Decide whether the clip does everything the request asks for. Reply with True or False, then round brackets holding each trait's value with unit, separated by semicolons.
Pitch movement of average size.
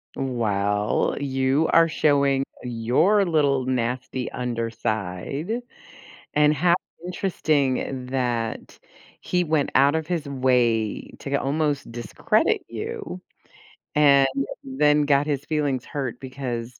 True (3.5 semitones)